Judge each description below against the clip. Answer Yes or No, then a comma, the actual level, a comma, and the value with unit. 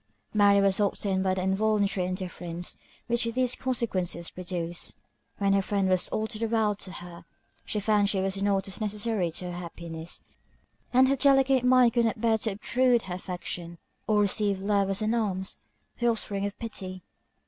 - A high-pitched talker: Yes, high, 200 Hz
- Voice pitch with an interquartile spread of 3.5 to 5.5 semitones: No, average, 3.1 semitones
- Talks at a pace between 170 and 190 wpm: Yes, average, 180 wpm